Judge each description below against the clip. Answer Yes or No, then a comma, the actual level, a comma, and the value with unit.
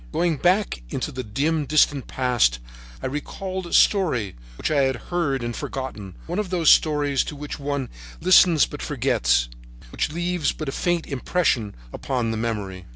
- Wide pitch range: Yes, wide, 6.2 semitones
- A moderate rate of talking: Yes, average, 170 wpm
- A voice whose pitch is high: No, medium, 140 Hz